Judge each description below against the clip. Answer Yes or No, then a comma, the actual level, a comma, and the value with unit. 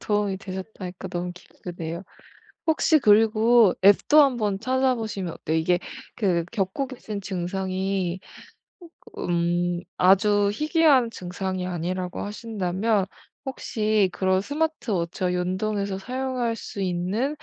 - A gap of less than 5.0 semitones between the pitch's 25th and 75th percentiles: Yes, average, 4.0 semitones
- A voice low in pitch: No, high, 195 Hz